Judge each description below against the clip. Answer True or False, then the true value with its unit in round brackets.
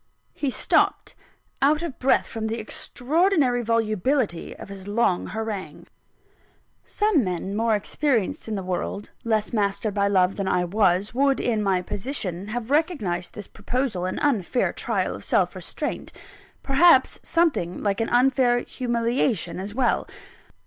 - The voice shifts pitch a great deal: False (4.9 semitones)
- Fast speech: False (140 wpm)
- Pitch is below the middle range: False (225 Hz)